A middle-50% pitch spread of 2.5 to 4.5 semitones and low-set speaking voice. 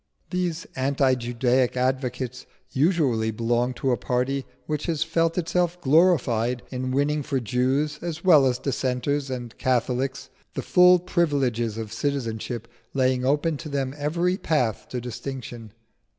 Yes: average, 3.5 semitones; low, 130 Hz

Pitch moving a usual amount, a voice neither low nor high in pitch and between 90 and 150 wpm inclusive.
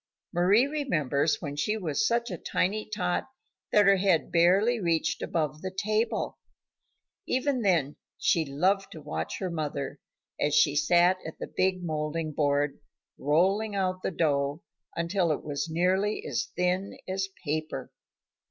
Yes: average, 4.4 semitones; medium, 175 Hz; average, 145 wpm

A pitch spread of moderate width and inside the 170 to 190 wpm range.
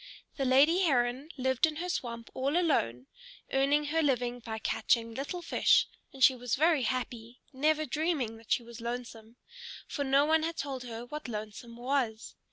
Yes: average, 4.1 semitones; average, 175 wpm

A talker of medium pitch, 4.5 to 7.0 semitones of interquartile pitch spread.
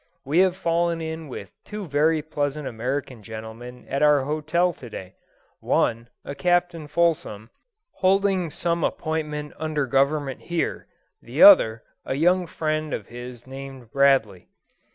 Yes: medium, 150 Hz; average, 4.8 semitones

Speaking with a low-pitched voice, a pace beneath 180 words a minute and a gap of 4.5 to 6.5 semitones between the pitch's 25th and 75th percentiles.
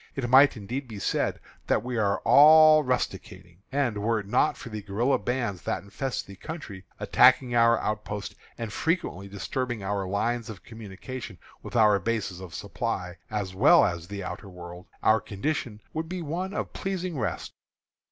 Yes: low, 110 Hz; average, 170 wpm; average, 5.0 semitones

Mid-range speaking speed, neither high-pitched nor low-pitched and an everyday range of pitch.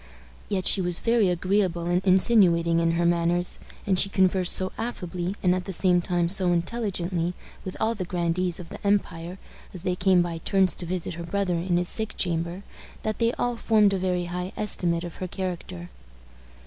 No: average, 190 wpm; medium, 180 Hz; narrow, 2.0 semitones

